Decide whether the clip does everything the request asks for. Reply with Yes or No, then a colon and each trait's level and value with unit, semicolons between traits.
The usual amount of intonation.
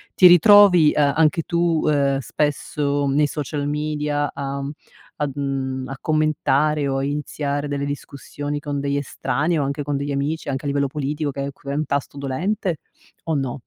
No: narrow, 1.6 semitones